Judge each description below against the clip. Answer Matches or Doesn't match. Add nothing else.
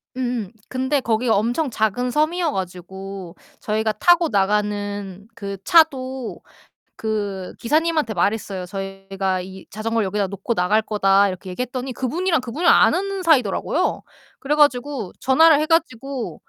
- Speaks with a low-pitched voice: Doesn't match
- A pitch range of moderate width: Doesn't match